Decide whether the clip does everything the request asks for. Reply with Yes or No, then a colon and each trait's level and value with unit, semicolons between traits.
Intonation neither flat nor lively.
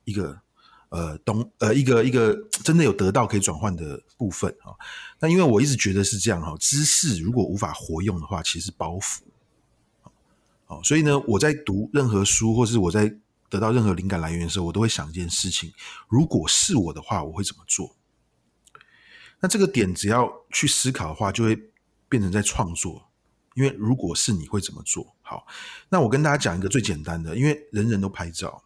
No: wide, 5.8 semitones